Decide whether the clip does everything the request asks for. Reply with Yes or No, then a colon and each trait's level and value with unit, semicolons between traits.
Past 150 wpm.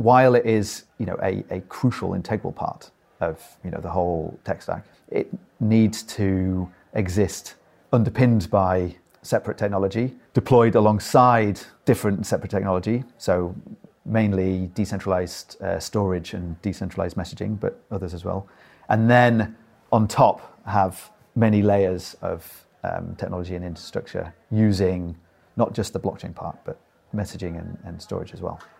No: average, 140 wpm